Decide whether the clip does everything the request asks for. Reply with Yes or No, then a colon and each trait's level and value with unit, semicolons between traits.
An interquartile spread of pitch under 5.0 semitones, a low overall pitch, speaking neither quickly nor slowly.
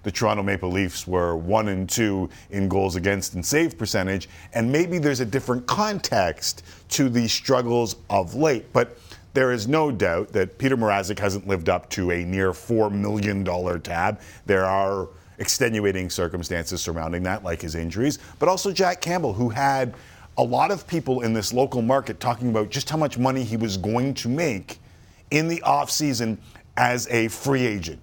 No: wide, 5.4 semitones; low, 110 Hz; average, 180 wpm